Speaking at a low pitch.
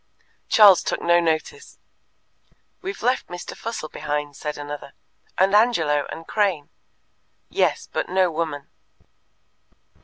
No: medium, 170 Hz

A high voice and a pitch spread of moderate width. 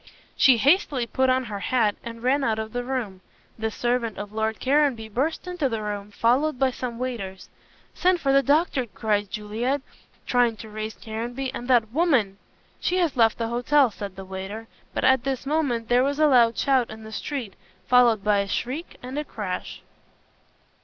Yes: high, 240 Hz; average, 3.7 semitones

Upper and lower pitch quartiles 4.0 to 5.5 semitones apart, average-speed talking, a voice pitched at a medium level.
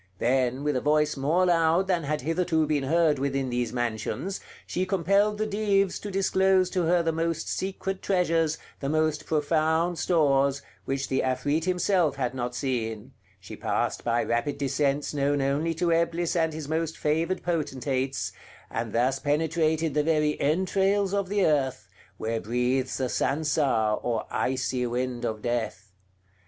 Yes: average, 4.3 semitones; average, 155 wpm; medium, 150 Hz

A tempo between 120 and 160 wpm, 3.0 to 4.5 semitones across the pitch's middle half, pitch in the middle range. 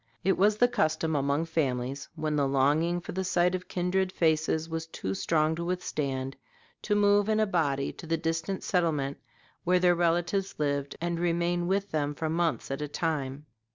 No: average, 185 wpm; average, 3.4 semitones; medium, 165 Hz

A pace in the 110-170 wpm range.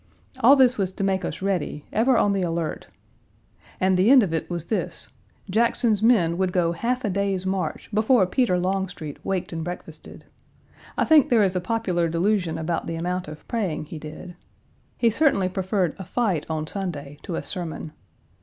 No: average, 180 wpm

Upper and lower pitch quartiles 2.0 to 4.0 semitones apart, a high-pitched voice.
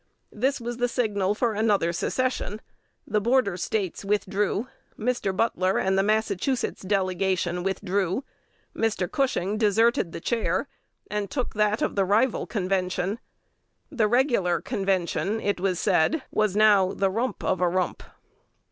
Yes: average, 3.3 semitones; high, 205 Hz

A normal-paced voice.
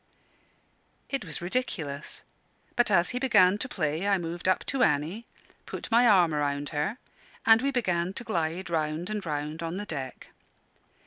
Yes: average, 165 wpm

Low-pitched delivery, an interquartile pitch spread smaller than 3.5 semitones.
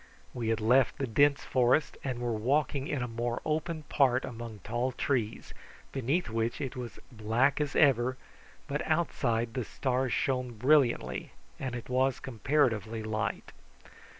Yes: low, 125 Hz; average, 3.1 semitones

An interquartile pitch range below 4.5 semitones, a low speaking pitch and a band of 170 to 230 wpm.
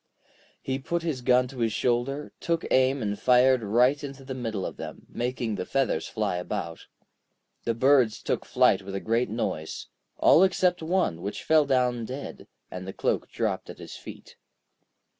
Yes: average, 4.0 semitones; low, 125 Hz; average, 175 wpm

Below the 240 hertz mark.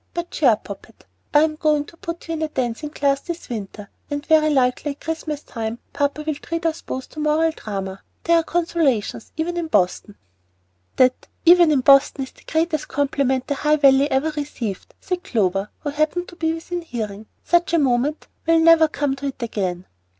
No: very high, 295 Hz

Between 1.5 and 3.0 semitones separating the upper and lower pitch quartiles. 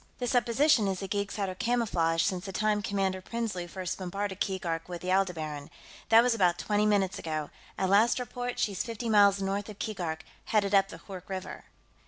Yes: narrow, 2.6 semitones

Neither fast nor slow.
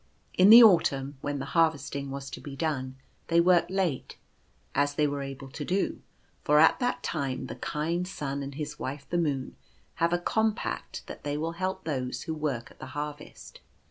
Yes: average, 190 wpm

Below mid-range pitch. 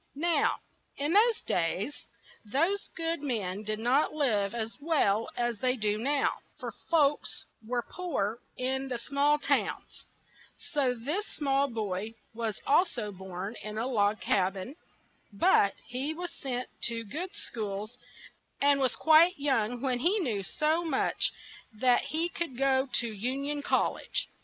No: very high, 255 Hz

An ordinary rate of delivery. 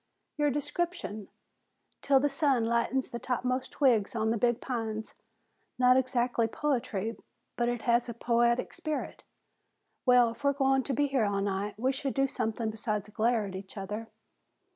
Yes: average, 165 wpm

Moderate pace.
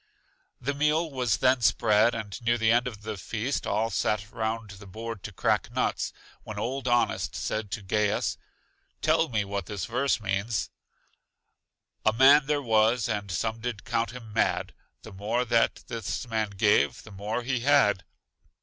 Yes: average, 165 wpm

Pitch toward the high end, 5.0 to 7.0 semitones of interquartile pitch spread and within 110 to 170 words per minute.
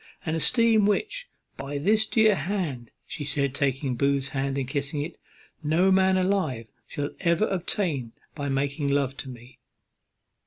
No: medium, 145 Hz; wide, 5.5 semitones; average, 150 wpm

